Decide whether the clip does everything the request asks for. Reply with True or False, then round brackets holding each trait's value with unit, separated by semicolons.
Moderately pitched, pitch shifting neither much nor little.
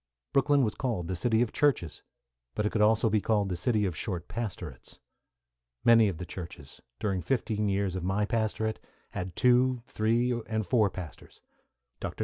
False (105 Hz; 4.0 semitones)